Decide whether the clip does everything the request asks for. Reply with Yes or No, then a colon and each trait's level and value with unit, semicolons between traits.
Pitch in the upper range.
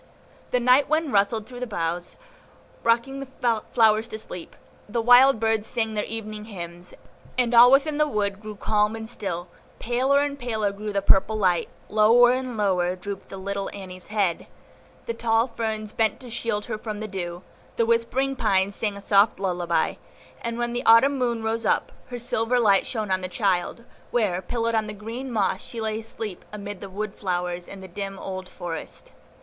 Yes: high, 215 Hz